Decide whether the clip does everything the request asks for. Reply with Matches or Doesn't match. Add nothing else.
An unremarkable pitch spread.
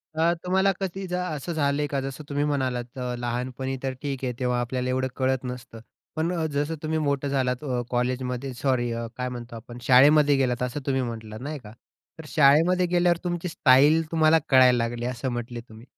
Matches